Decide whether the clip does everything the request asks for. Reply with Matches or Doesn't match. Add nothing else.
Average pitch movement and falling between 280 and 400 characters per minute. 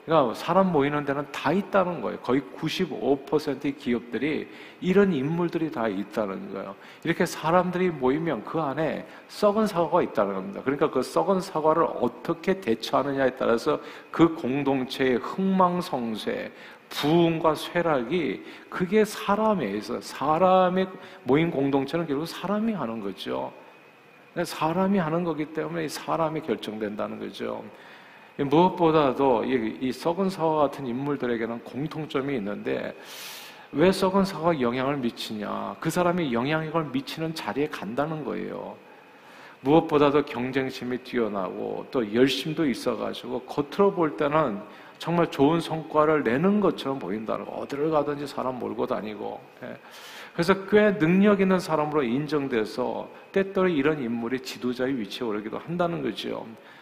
Matches